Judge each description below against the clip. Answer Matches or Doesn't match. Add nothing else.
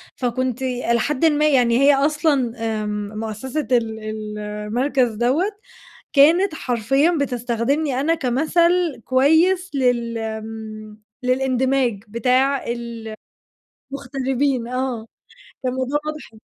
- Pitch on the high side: Matches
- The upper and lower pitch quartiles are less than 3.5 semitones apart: Doesn't match